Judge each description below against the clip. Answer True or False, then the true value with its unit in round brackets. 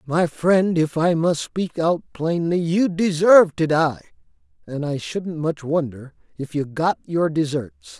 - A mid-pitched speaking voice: True (160 Hz)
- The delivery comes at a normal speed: True (160 wpm)